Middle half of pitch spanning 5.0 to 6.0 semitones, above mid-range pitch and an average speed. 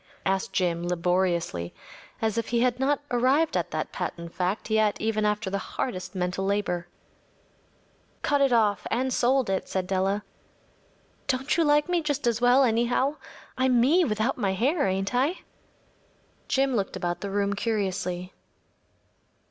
Yes: wide, 5.4 semitones; high, 215 Hz; average, 155 wpm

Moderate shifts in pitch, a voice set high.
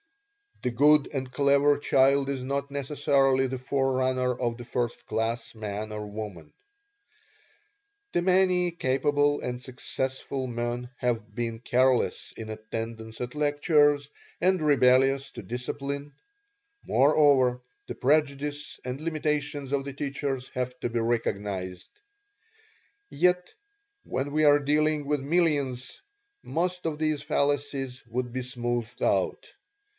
No: average, 3.0 semitones; low, 135 Hz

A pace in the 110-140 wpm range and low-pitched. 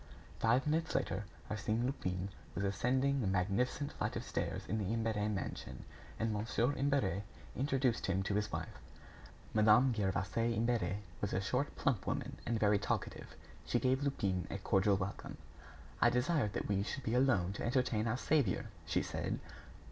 No: average, 165 wpm; low, 110 Hz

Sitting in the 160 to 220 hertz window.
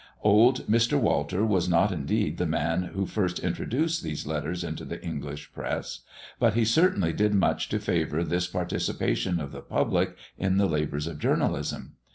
No: very low, 90 Hz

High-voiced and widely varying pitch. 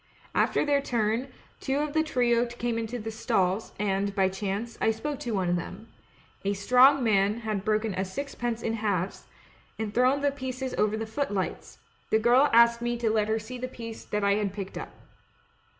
No: high, 225 Hz; average, 3.3 semitones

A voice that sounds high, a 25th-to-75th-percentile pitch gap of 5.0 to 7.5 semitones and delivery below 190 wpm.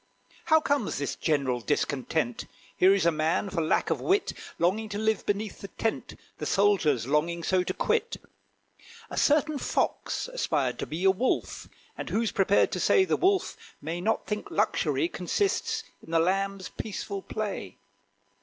Yes: high, 195 Hz; average, 5.3 semitones; average, 165 wpm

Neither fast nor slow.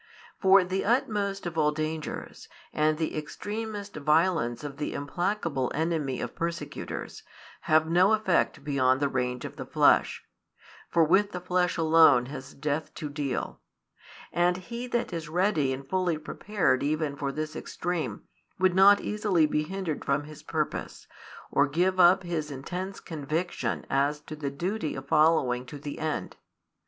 Yes: average, 155 wpm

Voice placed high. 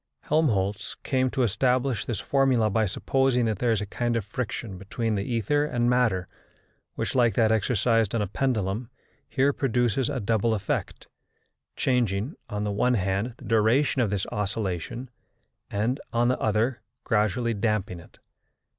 No: low, 115 Hz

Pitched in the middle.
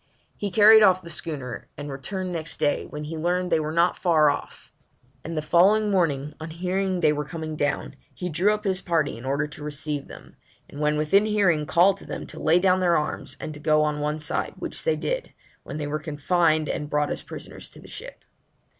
Yes: medium, 160 Hz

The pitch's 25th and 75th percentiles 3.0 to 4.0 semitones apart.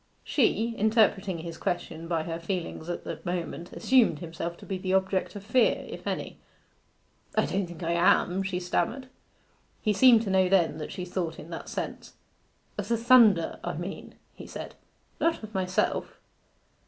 Yes: average, 3.7 semitones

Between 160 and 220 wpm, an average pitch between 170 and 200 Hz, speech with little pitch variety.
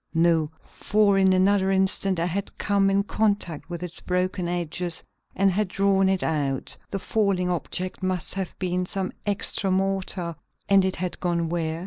Yes: average, 165 wpm; medium, 185 Hz; narrow, 2.0 semitones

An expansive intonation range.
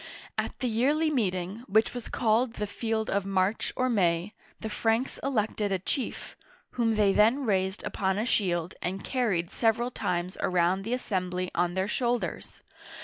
No: average, 4.1 semitones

